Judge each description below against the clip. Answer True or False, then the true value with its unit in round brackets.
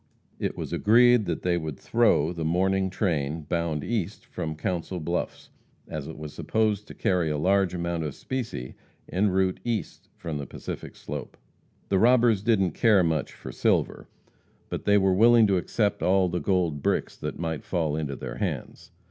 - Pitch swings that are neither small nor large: True (4.3 semitones)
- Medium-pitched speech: False (90 Hz)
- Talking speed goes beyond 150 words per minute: True (175 wpm)